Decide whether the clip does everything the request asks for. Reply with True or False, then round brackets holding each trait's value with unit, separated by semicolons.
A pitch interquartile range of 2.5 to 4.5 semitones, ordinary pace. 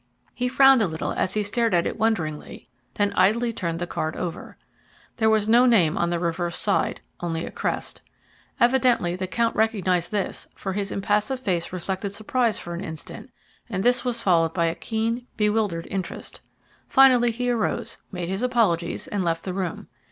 False (5.0 semitones; 180 wpm)